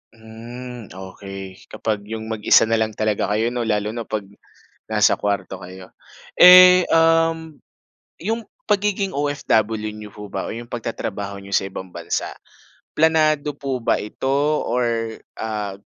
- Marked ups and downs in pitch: Yes, wide, 5.9 semitones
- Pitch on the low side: Yes, low, 110 Hz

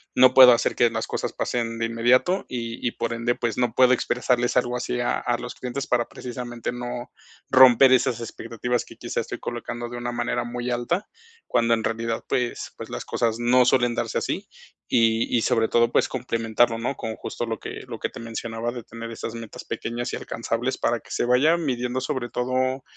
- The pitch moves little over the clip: Yes, narrow, 1.3 semitones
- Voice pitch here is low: Yes, low, 120 Hz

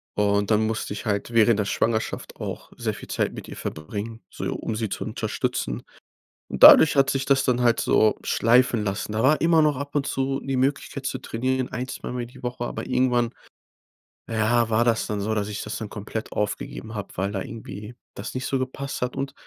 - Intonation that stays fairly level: No, average, 3.4 semitones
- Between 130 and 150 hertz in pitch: No, low, 115 Hz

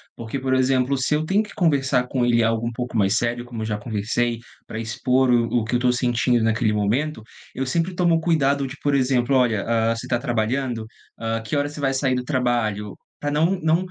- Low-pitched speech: Yes, low, 125 Hz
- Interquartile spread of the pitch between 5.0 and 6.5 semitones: No, average, 3.3 semitones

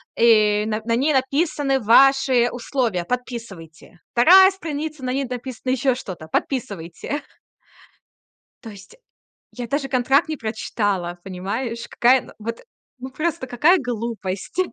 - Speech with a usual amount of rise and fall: Yes, average, 4.2 semitones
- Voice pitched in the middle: No, high, 245 Hz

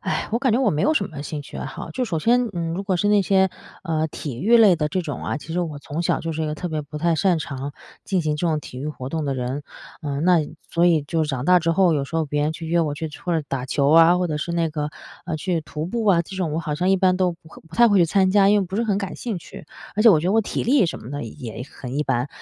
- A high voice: No, medium, 165 Hz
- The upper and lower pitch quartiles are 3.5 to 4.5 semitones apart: Yes, average, 4.1 semitones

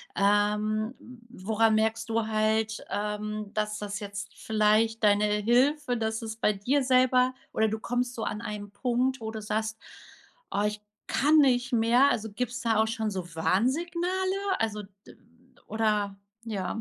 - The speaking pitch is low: No, high, 220 Hz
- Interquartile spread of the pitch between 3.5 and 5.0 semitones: No, average, 2.7 semitones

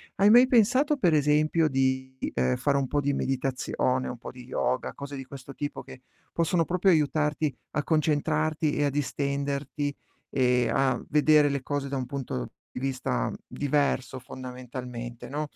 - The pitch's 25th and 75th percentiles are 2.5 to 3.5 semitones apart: Yes, average, 2.8 semitones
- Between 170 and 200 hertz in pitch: No, medium, 140 Hz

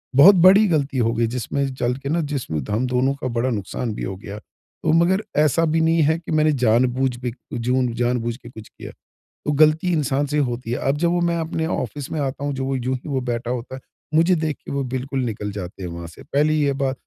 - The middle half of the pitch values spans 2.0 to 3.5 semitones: No, average, 4.2 semitones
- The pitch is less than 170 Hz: Yes, low, 135 Hz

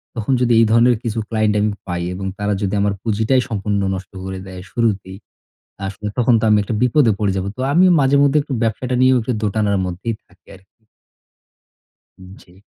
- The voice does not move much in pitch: No, average, 3.5 semitones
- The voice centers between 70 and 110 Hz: Yes, low, 105 Hz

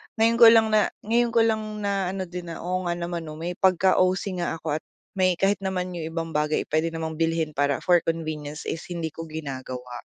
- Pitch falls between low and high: Yes, medium, 175 Hz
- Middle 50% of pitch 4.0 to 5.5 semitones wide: No, average, 3.1 semitones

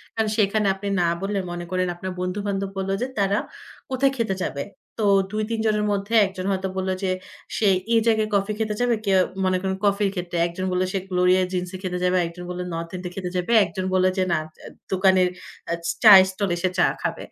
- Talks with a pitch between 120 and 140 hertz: No, high, 190 Hz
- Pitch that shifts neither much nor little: No, narrow, 2.2 semitones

